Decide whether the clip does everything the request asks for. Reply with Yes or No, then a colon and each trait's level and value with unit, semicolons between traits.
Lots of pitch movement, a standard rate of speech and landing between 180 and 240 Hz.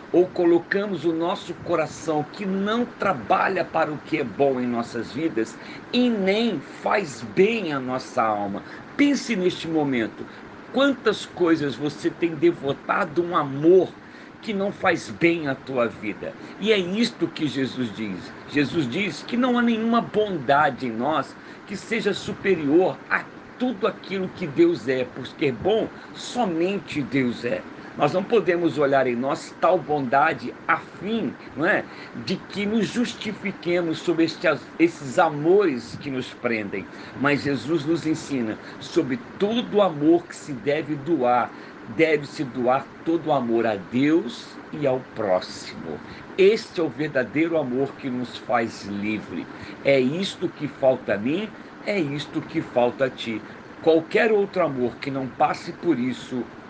No: wide, 6.8 semitones; average, 150 wpm; medium, 165 Hz